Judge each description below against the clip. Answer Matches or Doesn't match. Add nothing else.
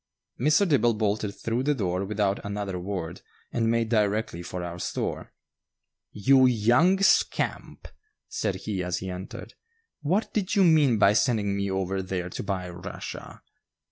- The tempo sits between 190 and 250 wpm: Doesn't match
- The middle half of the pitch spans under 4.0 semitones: Doesn't match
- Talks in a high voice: Doesn't match